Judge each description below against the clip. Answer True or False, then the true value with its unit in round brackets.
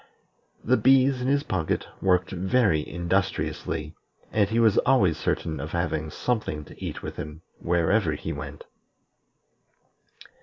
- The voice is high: False (90 Hz)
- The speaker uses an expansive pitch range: True (6.2 semitones)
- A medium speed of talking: False (130 wpm)